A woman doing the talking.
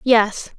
Yes: female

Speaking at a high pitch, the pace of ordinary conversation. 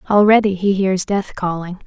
Yes: high, 195 Hz; average, 160 wpm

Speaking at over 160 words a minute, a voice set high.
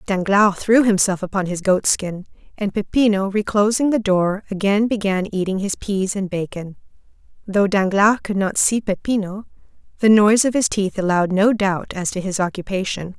Yes: average, 170 wpm; high, 200 Hz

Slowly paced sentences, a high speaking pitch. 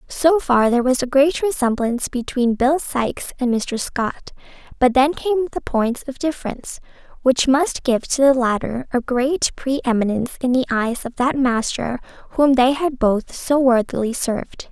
No: average, 175 wpm; very high, 260 Hz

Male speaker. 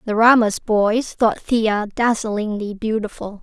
No: female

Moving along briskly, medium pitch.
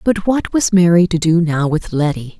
Yes: fast, 225 wpm; medium, 175 Hz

